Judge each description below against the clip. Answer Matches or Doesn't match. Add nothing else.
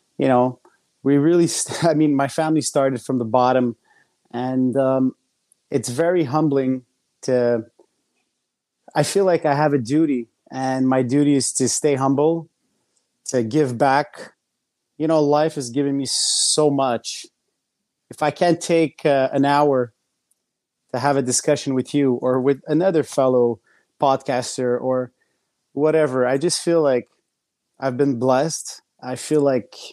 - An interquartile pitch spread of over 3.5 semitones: Doesn't match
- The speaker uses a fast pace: Doesn't match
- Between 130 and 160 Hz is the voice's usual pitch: Matches